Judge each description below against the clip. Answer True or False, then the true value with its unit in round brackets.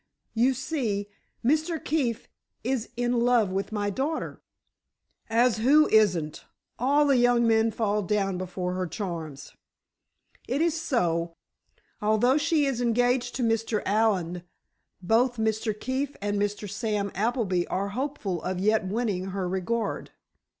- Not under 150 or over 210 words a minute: False (135 wpm)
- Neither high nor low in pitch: False (220 Hz)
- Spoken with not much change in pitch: False (4.1 semitones)